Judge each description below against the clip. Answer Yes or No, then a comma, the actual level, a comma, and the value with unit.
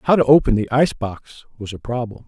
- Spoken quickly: Yes, fast, 235 wpm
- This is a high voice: No, low, 120 Hz